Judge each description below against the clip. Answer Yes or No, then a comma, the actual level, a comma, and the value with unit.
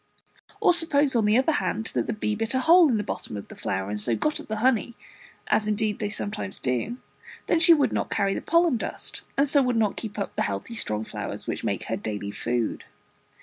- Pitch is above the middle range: Yes, high, 220 Hz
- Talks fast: Yes, fast, 230 wpm